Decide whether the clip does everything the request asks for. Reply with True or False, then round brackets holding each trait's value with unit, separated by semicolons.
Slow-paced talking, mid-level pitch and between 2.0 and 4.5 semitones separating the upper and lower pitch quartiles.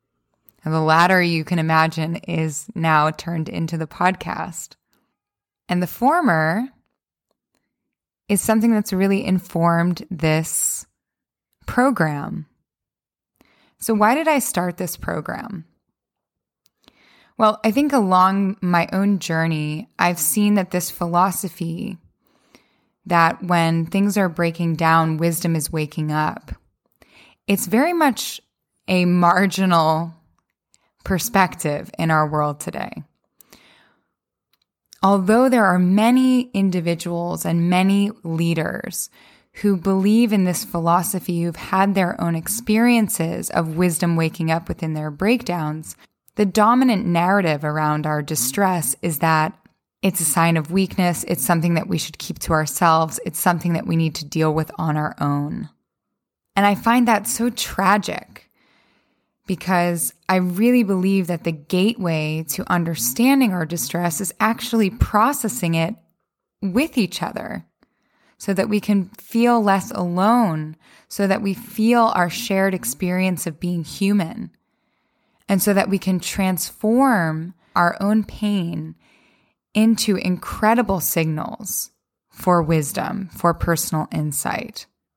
True (125 wpm; 180 Hz; 3.7 semitones)